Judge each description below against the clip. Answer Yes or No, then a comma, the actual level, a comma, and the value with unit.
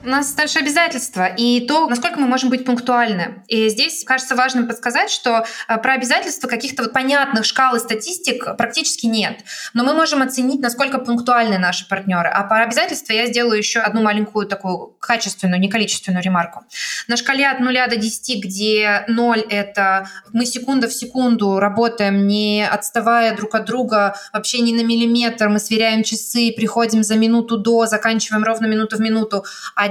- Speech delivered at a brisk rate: Yes, fast, 170 wpm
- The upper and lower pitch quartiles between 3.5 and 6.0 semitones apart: No, average, 2.9 semitones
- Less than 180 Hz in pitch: No, high, 230 Hz